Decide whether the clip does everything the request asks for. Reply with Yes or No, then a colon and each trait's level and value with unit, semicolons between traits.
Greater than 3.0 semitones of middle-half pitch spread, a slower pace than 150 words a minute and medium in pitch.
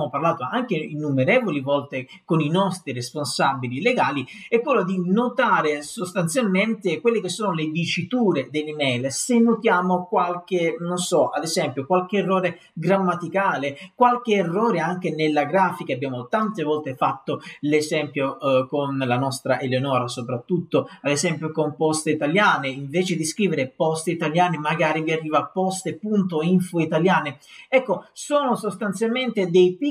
Yes: average, 4.5 semitones; average, 130 wpm; medium, 170 Hz